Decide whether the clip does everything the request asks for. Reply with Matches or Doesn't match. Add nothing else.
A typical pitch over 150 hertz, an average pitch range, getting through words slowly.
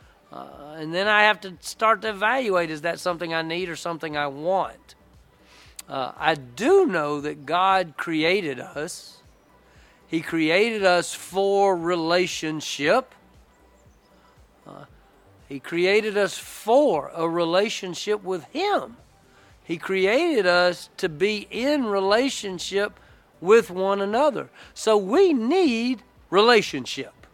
Matches